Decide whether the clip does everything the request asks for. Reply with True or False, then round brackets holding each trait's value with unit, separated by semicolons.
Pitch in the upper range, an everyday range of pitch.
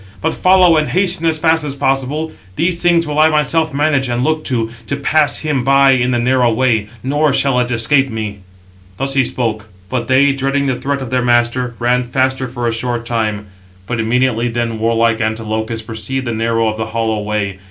False (125 Hz; 3.6 semitones)